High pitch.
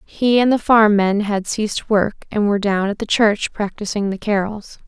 Yes: high, 210 Hz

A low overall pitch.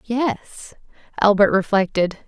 No: high, 210 Hz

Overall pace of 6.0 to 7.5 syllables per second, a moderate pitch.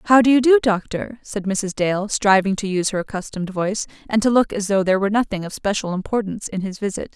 No: 6.5 syllables/s; high, 205 Hz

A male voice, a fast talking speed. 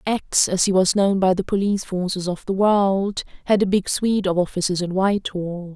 No: female; fast, 210 wpm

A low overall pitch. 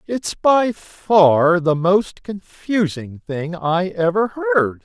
No: medium, 180 Hz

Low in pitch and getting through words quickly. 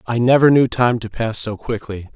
Yes: low, 115 Hz; fast, 225 wpm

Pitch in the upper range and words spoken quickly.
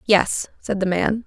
No: high, 200 Hz; average, 190 wpm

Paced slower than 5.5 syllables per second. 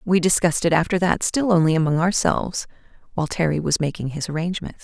No: 6.6 syllables/s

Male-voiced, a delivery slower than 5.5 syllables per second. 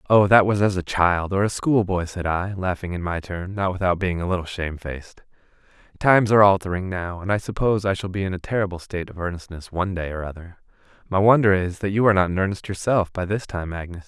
No: male; 6.4 syllables/s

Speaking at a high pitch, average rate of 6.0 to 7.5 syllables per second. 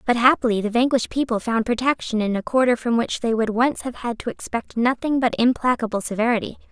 Yes: high, 235 Hz; 6.1 syllables/s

